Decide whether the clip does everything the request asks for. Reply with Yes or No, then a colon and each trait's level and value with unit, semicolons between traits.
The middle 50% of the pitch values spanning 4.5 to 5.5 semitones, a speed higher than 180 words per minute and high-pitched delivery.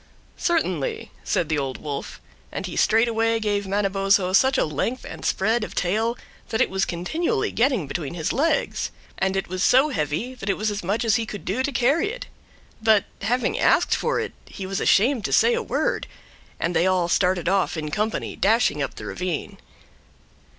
Yes: average, 4.9 semitones; average, 190 wpm; high, 205 Hz